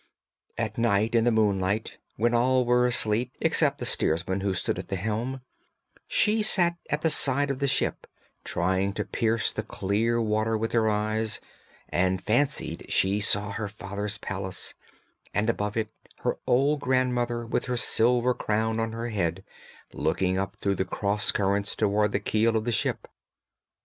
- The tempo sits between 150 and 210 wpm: Yes, average, 165 wpm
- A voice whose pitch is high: No, low, 110 Hz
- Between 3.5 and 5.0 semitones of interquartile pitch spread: No, average, 3.1 semitones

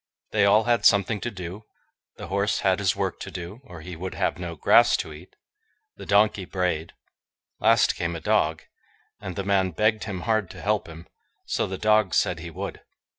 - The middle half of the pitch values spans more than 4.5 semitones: No, average, 3.3 semitones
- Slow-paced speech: No, average, 195 wpm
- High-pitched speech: No, very low, 95 Hz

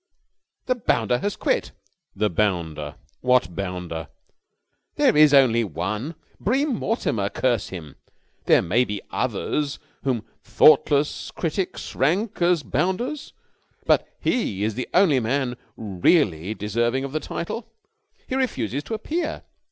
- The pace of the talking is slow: Yes, slow, 125 wpm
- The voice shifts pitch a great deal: Yes, wide, 9.0 semitones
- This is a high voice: No, low, 125 Hz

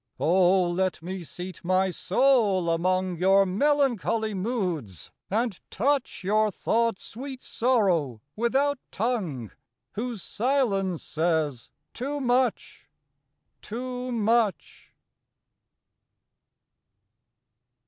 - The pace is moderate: No, slow, 85 wpm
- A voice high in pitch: Yes, high, 205 Hz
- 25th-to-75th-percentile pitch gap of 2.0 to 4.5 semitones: No, average, 5.2 semitones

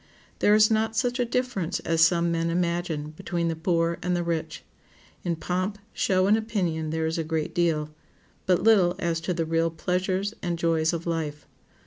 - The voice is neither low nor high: Yes, medium, 170 Hz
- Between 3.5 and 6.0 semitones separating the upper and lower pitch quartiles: No, narrow, 2.4 semitones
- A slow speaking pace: No, average, 185 wpm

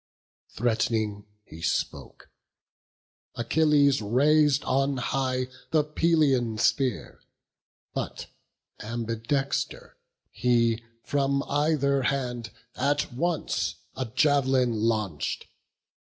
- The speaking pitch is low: Yes, low, 130 Hz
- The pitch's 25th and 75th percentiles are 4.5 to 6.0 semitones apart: No, average, 3.7 semitones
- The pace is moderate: No, slow, 80 wpm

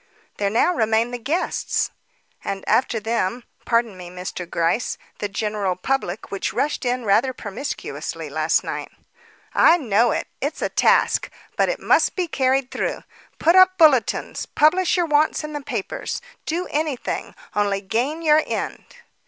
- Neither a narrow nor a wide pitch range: No, wide, 6.8 semitones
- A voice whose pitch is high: Yes, high, 245 Hz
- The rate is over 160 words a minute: No, average, 155 wpm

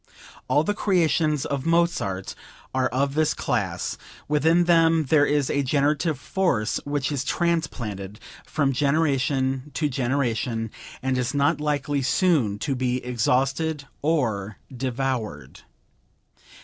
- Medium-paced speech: No, slow, 120 wpm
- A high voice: No, medium, 140 Hz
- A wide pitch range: No, average, 3.5 semitones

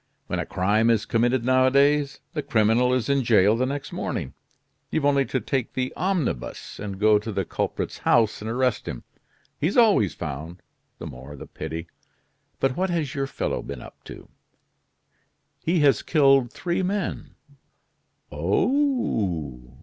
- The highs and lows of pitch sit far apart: Yes, wide, 5.7 semitones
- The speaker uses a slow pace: No, average, 150 wpm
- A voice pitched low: Yes, low, 125 Hz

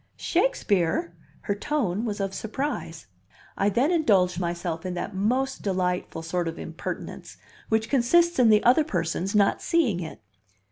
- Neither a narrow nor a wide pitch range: No, wide, 6.0 semitones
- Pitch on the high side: Yes, high, 200 Hz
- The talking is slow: No, average, 145 wpm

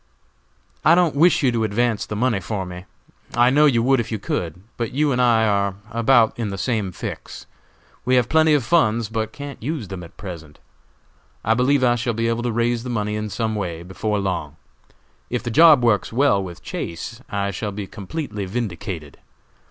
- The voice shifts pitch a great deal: No, average, 3.9 semitones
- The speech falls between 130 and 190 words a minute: No, average, 200 wpm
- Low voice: Yes, low, 115 Hz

